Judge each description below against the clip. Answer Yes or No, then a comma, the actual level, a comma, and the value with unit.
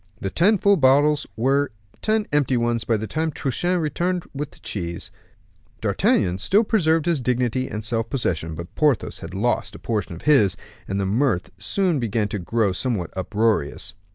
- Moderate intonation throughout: No, wide, 6.7 semitones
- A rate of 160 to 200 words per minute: Yes, average, 175 wpm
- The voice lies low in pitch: Yes, low, 125 Hz